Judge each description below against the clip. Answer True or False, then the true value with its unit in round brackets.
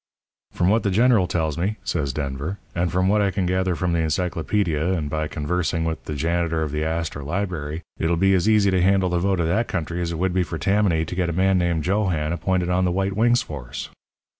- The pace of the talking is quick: True (235 wpm)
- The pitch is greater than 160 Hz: False (90 Hz)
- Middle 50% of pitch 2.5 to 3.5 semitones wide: True (2.9 semitones)